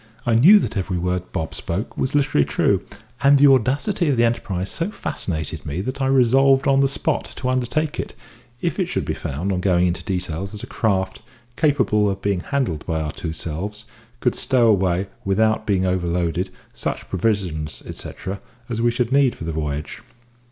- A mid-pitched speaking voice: No, low, 100 Hz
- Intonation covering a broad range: Yes, wide, 6.5 semitones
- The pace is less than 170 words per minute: No, average, 185 wpm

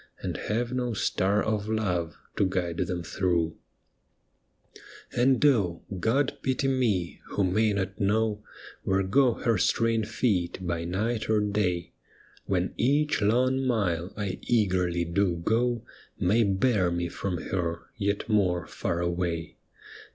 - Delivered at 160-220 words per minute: No, slow, 135 wpm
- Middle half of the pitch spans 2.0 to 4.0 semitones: No, average, 4.4 semitones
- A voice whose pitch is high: No, low, 100 Hz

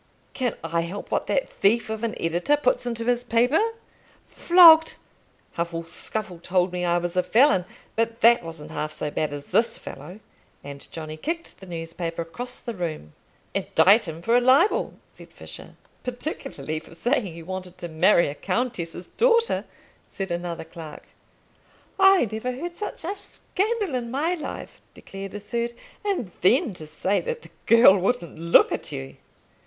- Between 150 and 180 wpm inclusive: Yes, average, 165 wpm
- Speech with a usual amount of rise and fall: No, wide, 6.8 semitones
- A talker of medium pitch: No, high, 200 Hz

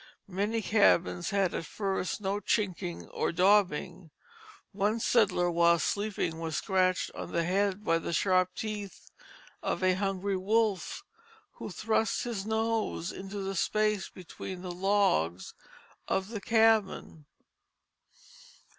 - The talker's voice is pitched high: Yes, high, 195 Hz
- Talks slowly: Yes, slow, 125 wpm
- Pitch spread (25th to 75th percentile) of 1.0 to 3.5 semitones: Yes, average, 2.8 semitones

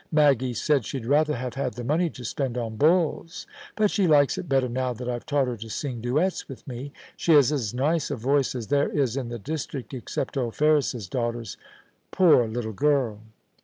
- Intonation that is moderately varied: Yes, average, 3.6 semitones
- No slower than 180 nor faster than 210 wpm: Yes, fast, 205 wpm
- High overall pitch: No, low, 135 Hz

